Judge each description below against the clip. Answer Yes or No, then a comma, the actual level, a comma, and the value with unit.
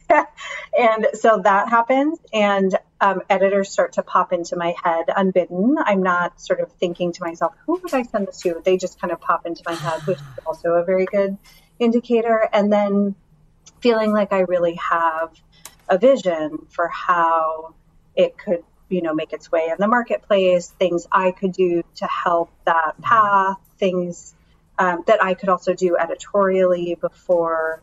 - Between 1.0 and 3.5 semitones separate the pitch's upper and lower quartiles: Yes, average, 3.0 semitones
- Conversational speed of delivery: Yes, average, 175 wpm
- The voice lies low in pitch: No, medium, 185 Hz